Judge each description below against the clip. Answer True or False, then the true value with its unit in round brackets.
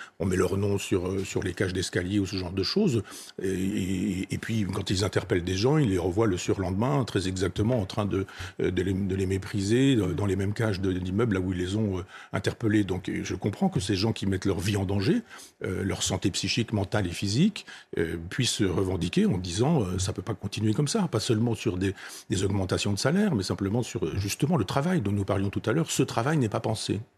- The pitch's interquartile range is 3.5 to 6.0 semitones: False (2.9 semitones)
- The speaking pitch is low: True (100 Hz)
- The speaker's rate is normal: False (240 wpm)